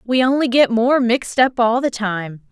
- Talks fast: Yes, fast, 215 wpm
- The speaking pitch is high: Yes, high, 240 Hz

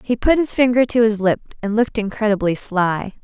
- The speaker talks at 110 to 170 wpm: No, fast, 205 wpm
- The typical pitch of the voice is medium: No, high, 220 Hz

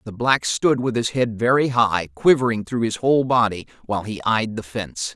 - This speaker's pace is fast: Yes, fast, 210 wpm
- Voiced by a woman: No, male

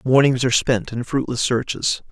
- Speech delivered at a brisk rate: No, average, 170 wpm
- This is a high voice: No, low, 125 Hz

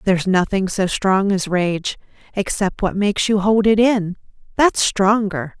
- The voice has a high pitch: Yes, high, 195 Hz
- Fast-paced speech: No, average, 150 wpm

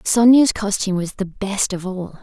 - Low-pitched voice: No, high, 200 Hz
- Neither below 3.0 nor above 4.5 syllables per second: No, 4.7 syllables/s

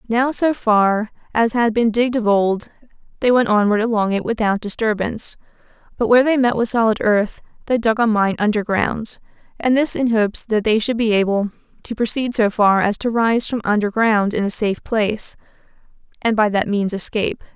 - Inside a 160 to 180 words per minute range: No, average, 195 wpm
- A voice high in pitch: Yes, high, 220 Hz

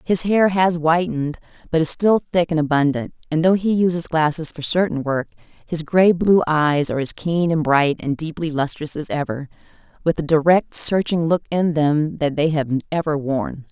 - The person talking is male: No, female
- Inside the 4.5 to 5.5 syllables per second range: Yes, 4.9 syllables/s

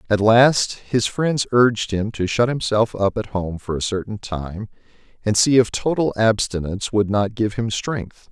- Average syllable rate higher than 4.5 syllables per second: No, 4.4 syllables/s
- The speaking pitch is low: Yes, low, 110 Hz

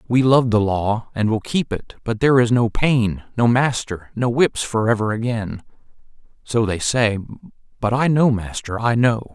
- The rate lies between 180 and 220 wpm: Yes, average, 185 wpm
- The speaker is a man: Yes, male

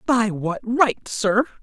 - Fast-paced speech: No, average, 150 wpm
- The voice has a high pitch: Yes, high, 225 Hz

